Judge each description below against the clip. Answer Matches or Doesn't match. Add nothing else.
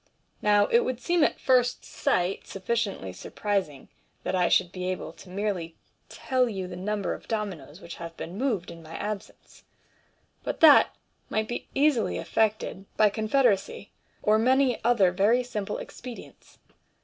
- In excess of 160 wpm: Doesn't match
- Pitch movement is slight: Doesn't match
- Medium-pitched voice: Doesn't match